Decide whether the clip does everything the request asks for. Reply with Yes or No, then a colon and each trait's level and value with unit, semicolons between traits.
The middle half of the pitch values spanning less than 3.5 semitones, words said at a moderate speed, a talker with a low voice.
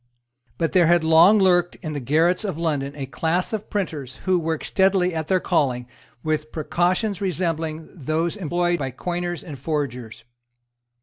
No: average, 2.9 semitones; average, 160 wpm; medium, 165 Hz